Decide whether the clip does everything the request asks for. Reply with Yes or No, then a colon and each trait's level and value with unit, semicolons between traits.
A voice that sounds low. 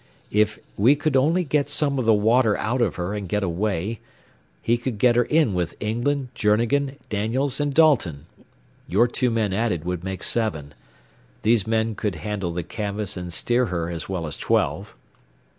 Yes: low, 110 Hz